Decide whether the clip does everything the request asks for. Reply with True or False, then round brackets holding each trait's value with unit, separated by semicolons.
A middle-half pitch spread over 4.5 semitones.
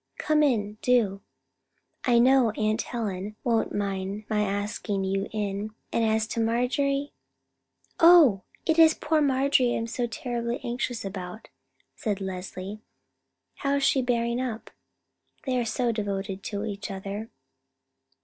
False (3.8 semitones)